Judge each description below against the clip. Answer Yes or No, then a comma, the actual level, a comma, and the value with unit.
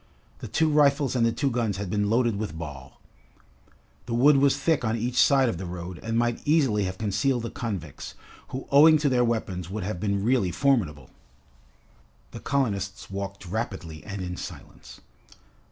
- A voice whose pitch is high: No, low, 110 Hz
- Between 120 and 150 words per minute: No, average, 175 wpm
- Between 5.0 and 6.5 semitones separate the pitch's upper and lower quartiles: Yes, wide, 5.5 semitones